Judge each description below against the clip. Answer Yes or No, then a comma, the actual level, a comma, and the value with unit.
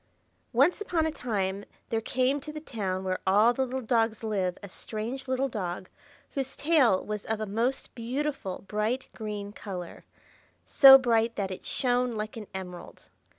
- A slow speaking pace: No, average, 160 wpm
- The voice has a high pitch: Yes, high, 225 Hz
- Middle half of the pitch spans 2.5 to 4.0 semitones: No, average, 4.5 semitones